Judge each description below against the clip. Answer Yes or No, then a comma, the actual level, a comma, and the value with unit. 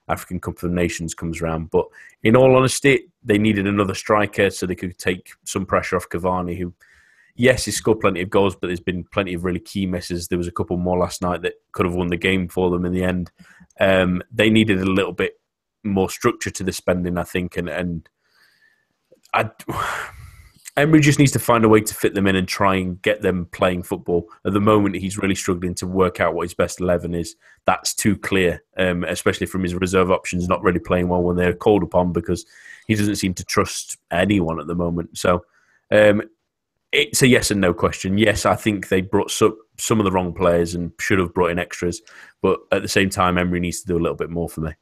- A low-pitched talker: Yes, very low, 95 Hz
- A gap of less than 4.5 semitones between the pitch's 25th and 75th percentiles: Yes, average, 2.7 semitones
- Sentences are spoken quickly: Yes, fast, 225 wpm